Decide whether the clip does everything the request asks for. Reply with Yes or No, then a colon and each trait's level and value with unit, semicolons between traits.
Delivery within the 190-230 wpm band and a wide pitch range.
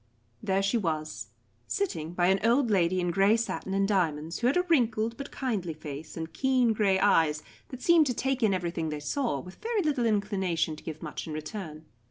Yes: fast, 205 wpm; wide, 6.7 semitones